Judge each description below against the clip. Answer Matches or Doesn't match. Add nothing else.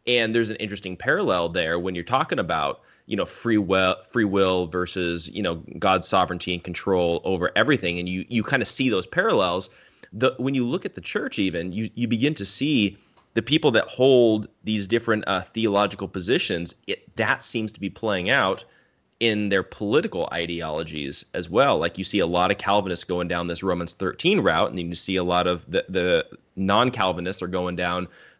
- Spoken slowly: Doesn't match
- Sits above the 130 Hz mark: Doesn't match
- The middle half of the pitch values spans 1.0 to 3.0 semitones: Doesn't match